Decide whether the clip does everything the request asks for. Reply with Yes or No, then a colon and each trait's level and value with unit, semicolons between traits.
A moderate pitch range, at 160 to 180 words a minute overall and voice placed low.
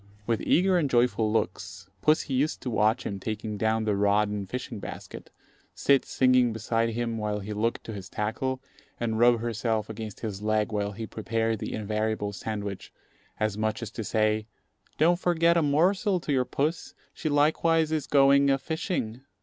Yes: average, 4.4 semitones; average, 175 wpm; low, 115 Hz